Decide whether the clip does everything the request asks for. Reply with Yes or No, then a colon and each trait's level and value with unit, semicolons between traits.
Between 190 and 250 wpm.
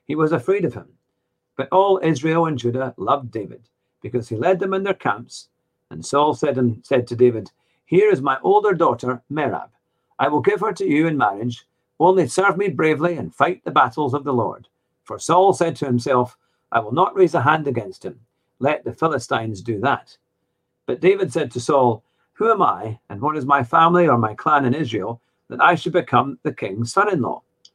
Yes: fast, 205 wpm